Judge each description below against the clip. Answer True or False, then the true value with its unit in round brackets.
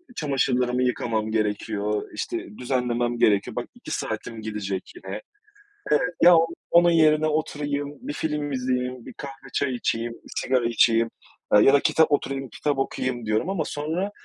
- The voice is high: False (125 Hz)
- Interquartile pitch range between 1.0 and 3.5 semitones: False (4.4 semitones)